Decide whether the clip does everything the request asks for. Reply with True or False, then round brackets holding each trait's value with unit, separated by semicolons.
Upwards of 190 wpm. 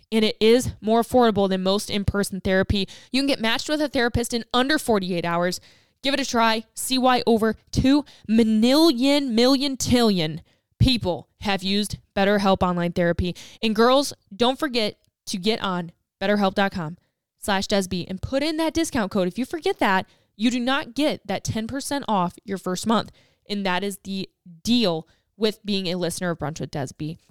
False (175 wpm)